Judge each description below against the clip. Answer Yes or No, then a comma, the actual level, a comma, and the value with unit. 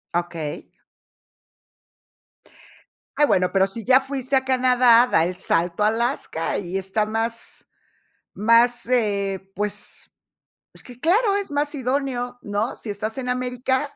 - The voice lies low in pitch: No, high, 235 Hz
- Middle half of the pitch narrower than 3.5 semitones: No, average, 4.5 semitones